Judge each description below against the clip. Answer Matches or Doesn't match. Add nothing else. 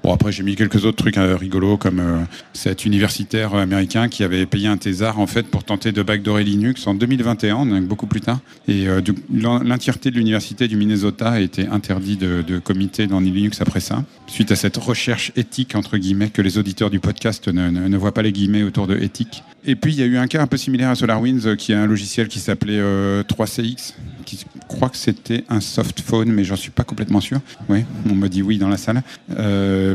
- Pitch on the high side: Doesn't match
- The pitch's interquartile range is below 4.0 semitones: Matches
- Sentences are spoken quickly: Matches